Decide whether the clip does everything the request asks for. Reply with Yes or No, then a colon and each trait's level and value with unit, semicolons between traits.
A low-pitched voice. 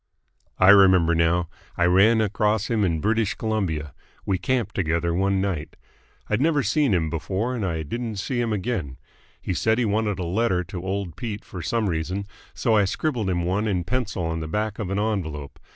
Yes: low, 100 Hz